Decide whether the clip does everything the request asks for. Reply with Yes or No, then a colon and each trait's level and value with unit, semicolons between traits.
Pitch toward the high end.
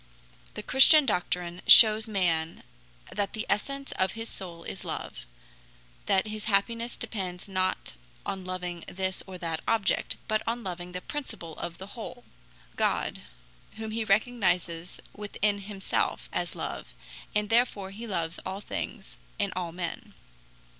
Yes: high, 195 Hz